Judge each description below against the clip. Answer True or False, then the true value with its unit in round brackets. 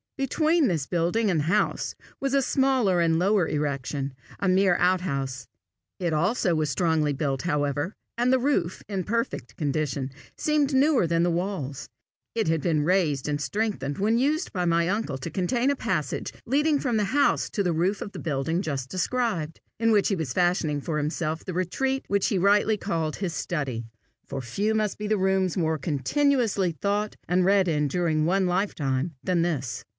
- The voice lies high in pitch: False (180 Hz)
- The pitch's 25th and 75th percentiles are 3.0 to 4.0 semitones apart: False (5.6 semitones)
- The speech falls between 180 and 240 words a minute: True (185 wpm)